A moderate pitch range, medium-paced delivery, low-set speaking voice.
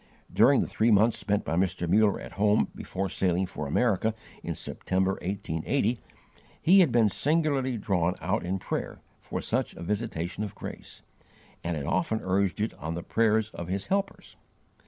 Yes: average, 4.0 semitones; average, 170 wpm; low, 100 Hz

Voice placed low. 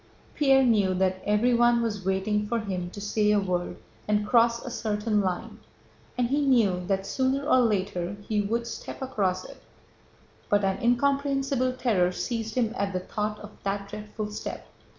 No: high, 210 Hz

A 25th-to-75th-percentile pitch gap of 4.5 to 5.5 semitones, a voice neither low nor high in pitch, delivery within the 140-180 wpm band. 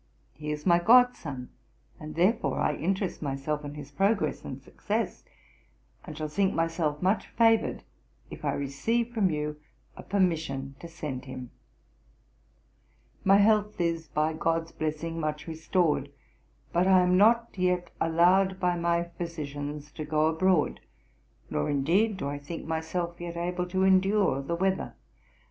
No: average, 3.8 semitones; medium, 170 Hz; average, 150 wpm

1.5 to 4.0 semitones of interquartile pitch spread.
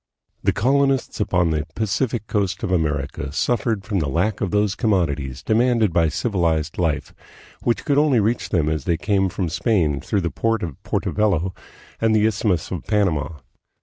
No: average, 5.2 semitones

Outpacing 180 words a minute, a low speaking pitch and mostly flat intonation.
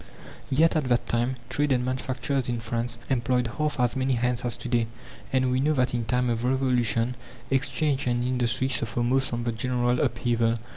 Yes: average, 190 wpm; low, 125 Hz; narrow, 1.7 semitones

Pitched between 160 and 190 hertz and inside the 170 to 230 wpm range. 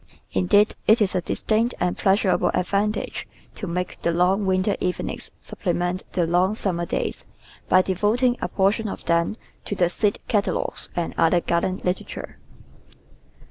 No: medium, 185 Hz; average, 150 wpm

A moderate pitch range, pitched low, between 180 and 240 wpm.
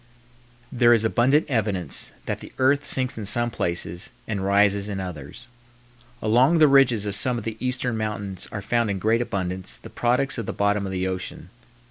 Yes: average, 4.0 semitones; low, 110 Hz; average, 185 wpm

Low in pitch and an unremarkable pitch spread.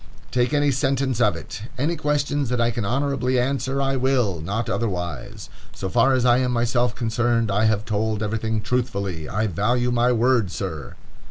Yes: low, 120 Hz; average, 3.3 semitones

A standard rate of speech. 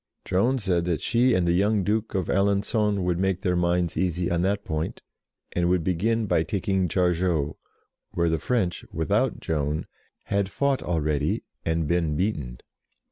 Yes: average, 160 wpm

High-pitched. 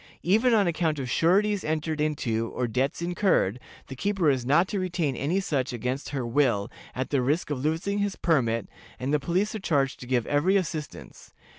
No: medium, 150 Hz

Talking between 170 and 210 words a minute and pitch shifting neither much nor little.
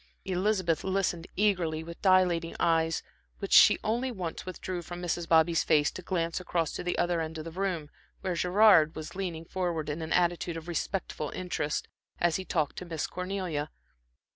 No: average, 180 wpm; narrow, 2.3 semitones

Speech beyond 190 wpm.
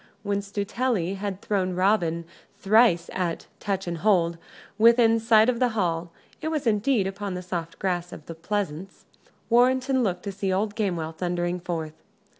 No: average, 160 wpm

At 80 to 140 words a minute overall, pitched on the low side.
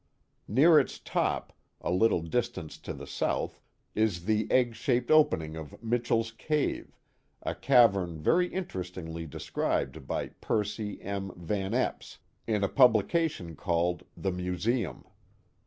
Yes: slow, 135 wpm; low, 105 Hz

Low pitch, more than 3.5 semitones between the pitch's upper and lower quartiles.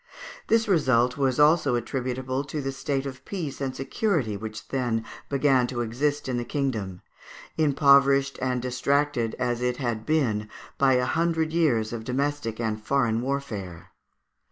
No: low, 130 Hz; average, 3.1 semitones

